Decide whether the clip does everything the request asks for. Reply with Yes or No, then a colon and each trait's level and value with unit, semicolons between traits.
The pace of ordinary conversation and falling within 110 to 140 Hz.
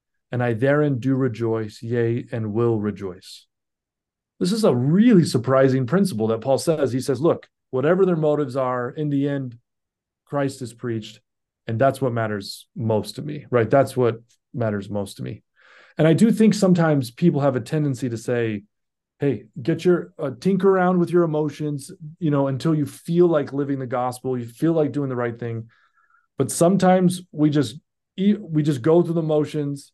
Yes: average, 180 wpm; low, 135 Hz